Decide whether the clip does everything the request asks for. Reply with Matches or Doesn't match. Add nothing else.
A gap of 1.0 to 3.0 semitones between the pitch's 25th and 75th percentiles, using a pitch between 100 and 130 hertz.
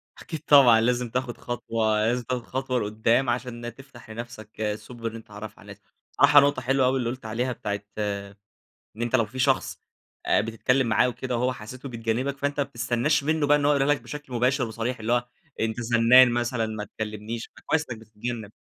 Matches